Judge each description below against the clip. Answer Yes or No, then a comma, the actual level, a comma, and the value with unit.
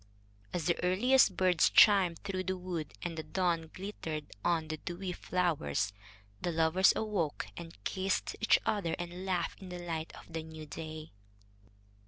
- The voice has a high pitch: No, medium, 175 Hz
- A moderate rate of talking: Yes, average, 160 wpm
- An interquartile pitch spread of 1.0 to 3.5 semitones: Yes, narrow, 2.6 semitones